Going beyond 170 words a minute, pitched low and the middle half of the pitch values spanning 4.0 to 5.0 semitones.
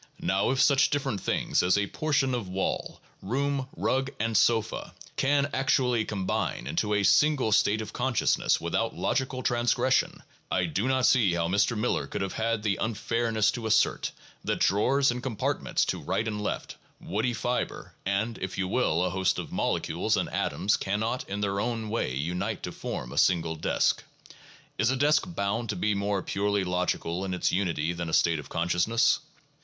Yes: average, 180 wpm; low, 105 Hz; average, 4.6 semitones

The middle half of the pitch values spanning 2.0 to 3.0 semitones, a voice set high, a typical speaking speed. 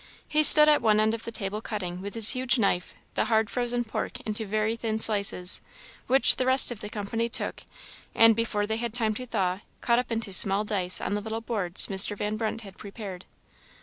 No: narrow, 2.4 semitones; high, 220 Hz; fast, 215 wpm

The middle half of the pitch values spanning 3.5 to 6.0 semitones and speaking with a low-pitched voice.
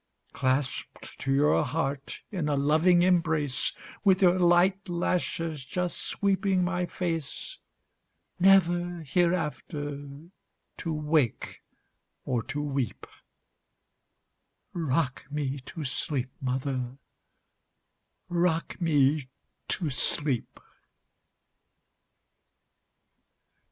No: average, 4.2 semitones; medium, 155 Hz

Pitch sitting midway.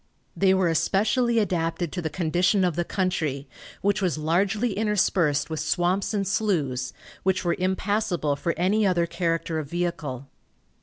Yes: medium, 175 Hz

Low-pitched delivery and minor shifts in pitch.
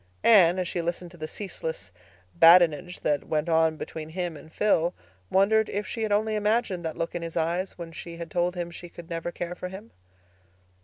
No: medium, 175 Hz; narrow, 2.3 semitones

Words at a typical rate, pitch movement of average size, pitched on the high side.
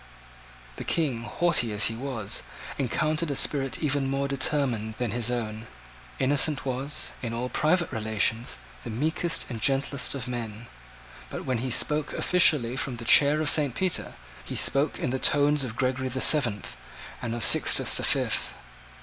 No: average, 165 wpm; average, 3.8 semitones; low, 130 Hz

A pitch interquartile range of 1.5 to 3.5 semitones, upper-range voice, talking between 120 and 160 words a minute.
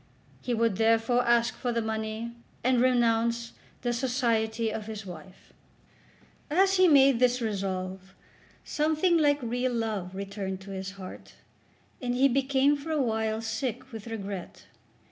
Yes: average, 3.0 semitones; high, 230 Hz; average, 145 wpm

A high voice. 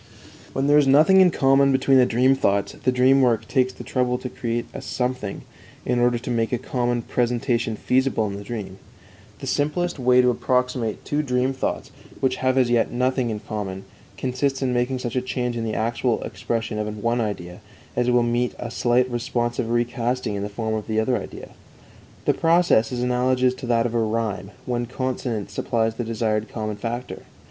No: low, 120 Hz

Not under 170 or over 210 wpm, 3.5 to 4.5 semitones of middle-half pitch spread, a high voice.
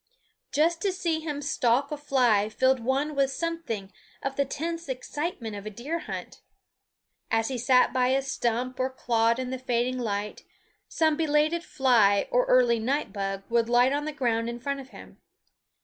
Yes: average, 180 wpm; average, 4.1 semitones; very high, 260 Hz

